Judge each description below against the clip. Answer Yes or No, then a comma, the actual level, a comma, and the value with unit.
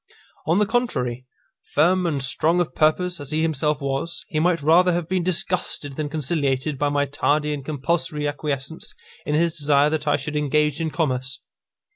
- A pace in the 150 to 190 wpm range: Yes, average, 175 wpm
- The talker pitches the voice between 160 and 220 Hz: No, medium, 150 Hz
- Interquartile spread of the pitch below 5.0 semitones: Yes, average, 2.8 semitones